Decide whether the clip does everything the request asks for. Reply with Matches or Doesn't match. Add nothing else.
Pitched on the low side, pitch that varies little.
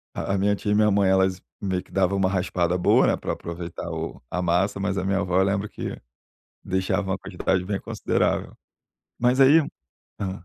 Matches